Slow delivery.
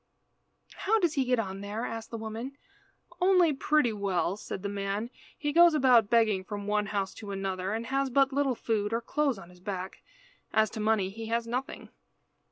No: average, 190 wpm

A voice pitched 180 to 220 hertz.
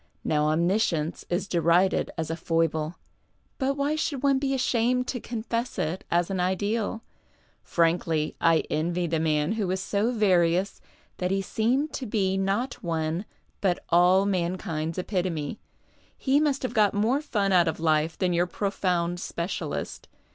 Yes: medium, 185 Hz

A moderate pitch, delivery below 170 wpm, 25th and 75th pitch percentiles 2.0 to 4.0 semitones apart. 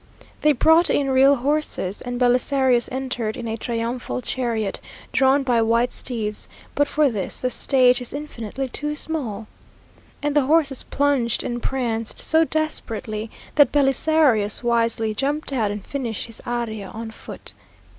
No: very high, 250 Hz; average, 145 wpm; average, 3.7 semitones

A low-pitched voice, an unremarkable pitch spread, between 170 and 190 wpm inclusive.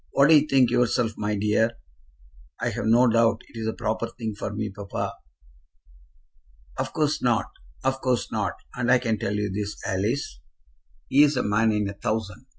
Yes: low, 115 Hz; average, 3.2 semitones; average, 175 wpm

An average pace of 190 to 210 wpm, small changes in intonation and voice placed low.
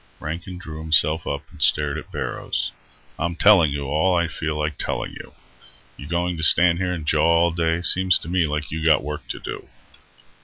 Yes: average, 200 wpm; narrow, 2.1 semitones; very low, 80 Hz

